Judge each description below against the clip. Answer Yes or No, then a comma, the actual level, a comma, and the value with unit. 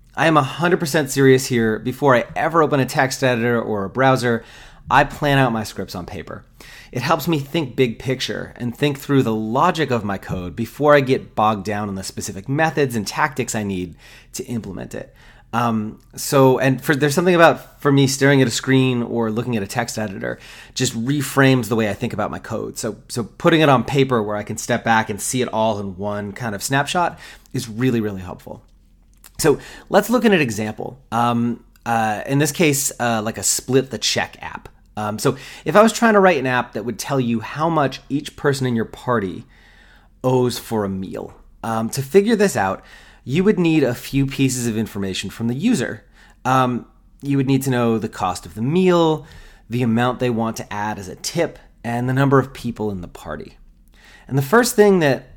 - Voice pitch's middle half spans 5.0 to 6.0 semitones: No, average, 4.1 semitones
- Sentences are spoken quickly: Yes, fast, 210 wpm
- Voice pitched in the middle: No, low, 125 Hz